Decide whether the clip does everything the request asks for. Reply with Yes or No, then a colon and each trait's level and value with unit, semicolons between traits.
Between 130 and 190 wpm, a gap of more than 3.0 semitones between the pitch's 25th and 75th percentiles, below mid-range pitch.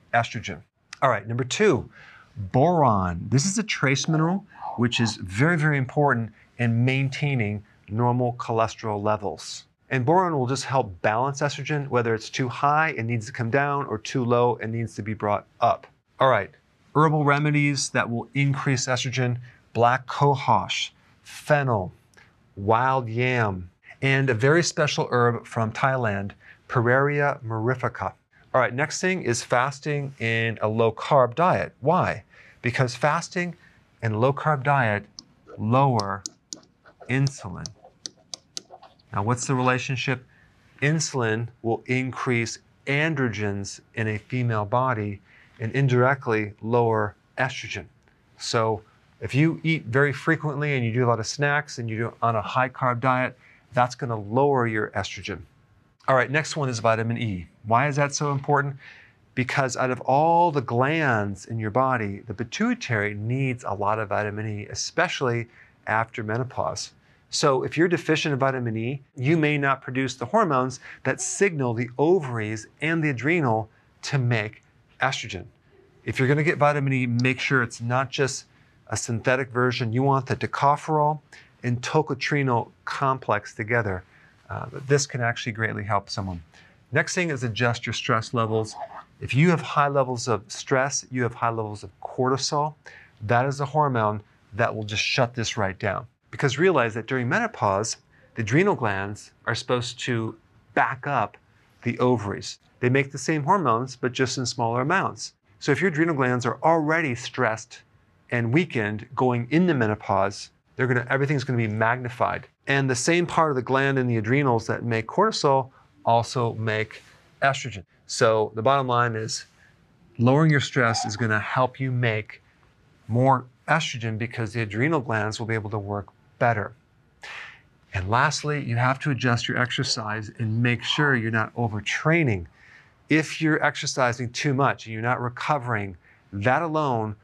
Yes: average, 155 wpm; average, 3.7 semitones; low, 125 Hz